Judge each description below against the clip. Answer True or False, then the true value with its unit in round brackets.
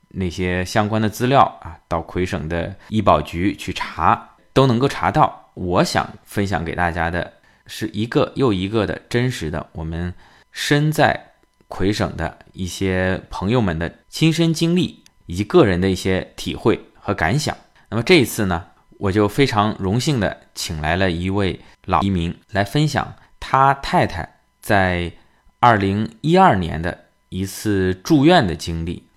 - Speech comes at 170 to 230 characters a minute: True (225 characters per minute)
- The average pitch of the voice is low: True (100 Hz)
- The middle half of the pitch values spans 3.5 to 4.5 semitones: False (5.3 semitones)